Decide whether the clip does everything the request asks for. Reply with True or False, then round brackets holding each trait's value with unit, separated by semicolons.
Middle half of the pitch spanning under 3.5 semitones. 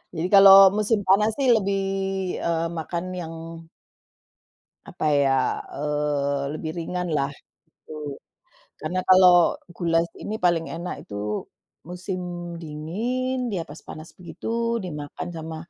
False (4.0 semitones)